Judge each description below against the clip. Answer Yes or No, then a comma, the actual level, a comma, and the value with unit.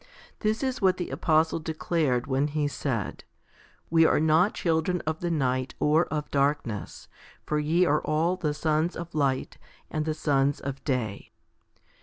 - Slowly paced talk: No, average, 165 wpm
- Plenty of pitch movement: No, average, 2.8 semitones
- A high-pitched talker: No, medium, 155 Hz